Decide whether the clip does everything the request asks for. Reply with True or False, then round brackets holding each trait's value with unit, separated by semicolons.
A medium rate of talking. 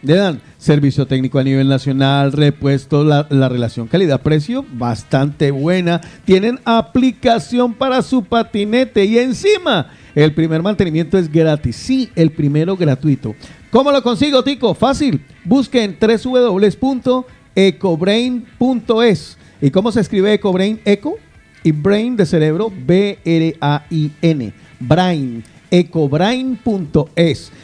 False (120 wpm)